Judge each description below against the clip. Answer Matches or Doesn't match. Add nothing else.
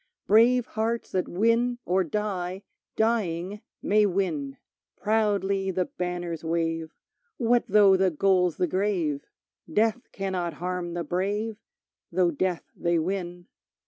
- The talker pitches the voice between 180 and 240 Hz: Matches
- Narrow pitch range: Doesn't match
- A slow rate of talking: Matches